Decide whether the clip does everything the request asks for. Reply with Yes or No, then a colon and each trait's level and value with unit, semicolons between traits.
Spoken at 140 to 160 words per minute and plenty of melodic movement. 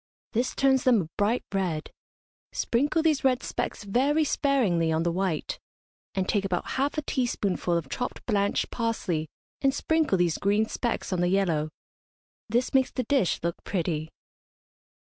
Yes: average, 155 wpm; wide, 6.9 semitones